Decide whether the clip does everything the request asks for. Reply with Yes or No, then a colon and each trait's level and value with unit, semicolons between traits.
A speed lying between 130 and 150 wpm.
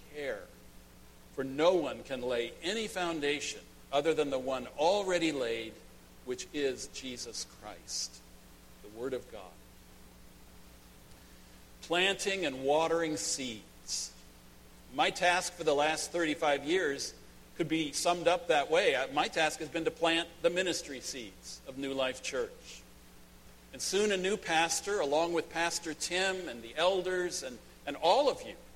Yes: average, 145 wpm